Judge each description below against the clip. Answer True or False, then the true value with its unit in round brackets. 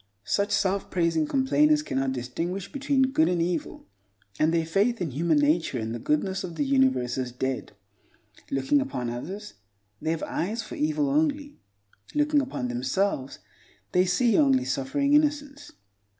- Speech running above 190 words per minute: False (150 wpm)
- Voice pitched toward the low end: False (190 Hz)